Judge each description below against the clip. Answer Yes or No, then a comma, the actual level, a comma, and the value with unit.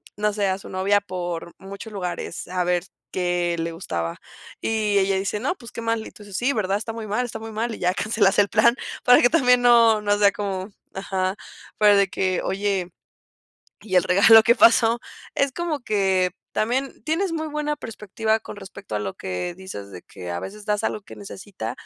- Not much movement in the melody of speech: No, average, 3.4 semitones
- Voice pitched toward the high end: Yes, high, 205 Hz